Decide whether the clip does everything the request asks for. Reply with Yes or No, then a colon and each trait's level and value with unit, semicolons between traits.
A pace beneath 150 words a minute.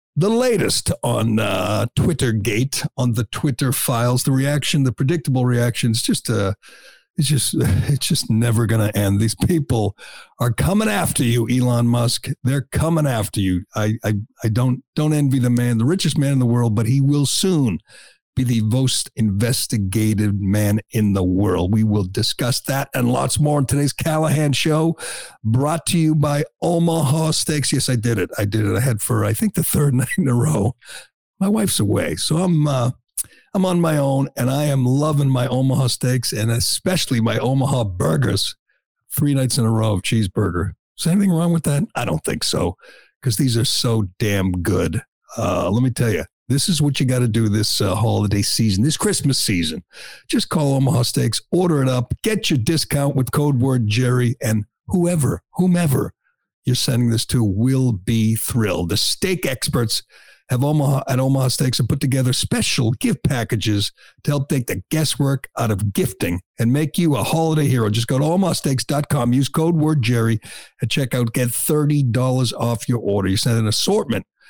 No: average, 190 wpm